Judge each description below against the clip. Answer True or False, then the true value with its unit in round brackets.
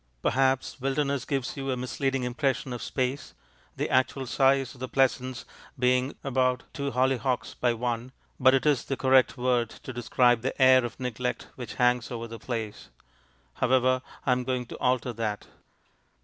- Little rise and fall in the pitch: True (1.4 semitones)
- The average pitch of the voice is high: False (130 Hz)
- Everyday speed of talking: True (165 wpm)